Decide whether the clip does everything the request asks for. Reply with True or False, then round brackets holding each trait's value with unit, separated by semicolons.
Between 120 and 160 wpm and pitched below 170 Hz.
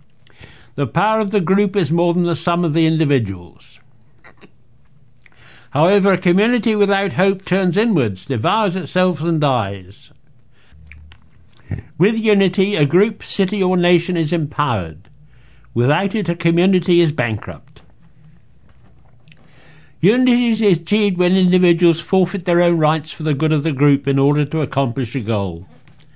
True (140 wpm; 160 Hz)